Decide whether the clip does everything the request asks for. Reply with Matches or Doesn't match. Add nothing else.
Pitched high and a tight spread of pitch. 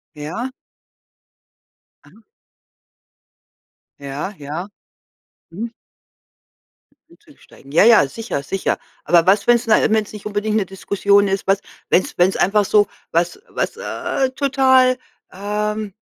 Doesn't match